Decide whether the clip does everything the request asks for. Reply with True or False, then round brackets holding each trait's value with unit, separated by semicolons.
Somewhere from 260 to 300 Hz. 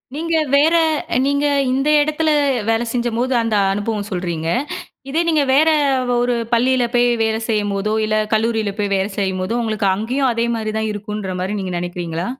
False (220 Hz)